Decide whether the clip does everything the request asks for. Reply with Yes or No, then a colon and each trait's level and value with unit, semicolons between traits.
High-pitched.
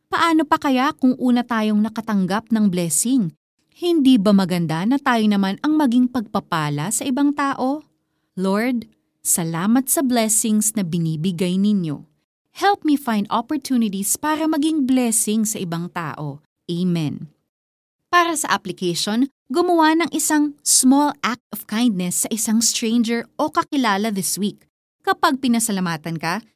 Yes: high, 225 Hz